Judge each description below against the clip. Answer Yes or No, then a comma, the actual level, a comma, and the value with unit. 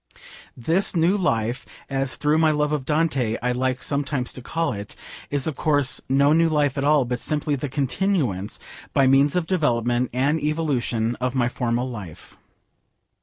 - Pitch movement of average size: Yes, average, 3.7 semitones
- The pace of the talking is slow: No, average, 170 wpm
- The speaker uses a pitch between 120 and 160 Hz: Yes, low, 135 Hz